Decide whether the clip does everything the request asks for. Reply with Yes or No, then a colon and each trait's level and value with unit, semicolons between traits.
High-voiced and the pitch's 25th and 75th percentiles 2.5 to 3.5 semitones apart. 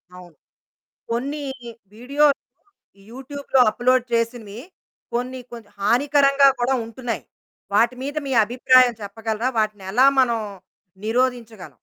Yes: high, 245 Hz; average, 2.8 semitones